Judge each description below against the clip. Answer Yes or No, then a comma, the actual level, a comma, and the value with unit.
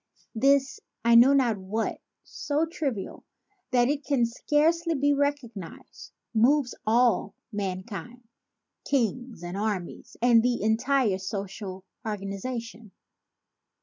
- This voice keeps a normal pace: No, slow, 105 wpm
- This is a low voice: No, high, 235 Hz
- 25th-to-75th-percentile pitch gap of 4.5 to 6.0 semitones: Yes, average, 5.1 semitones